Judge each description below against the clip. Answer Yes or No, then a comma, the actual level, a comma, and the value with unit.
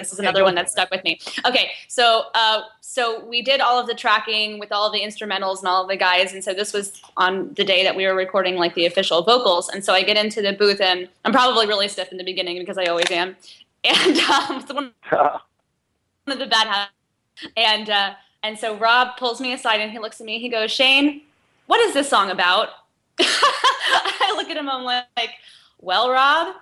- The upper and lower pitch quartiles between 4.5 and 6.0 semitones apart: No, average, 4.1 semitones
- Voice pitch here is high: Yes, high, 210 Hz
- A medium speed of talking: No, fast, 225 wpm